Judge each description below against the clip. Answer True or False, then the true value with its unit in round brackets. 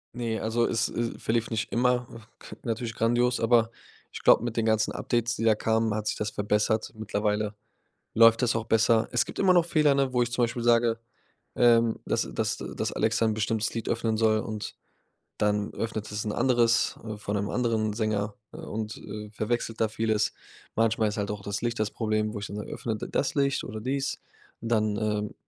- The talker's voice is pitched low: True (110 Hz)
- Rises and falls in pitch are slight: True (1.7 semitones)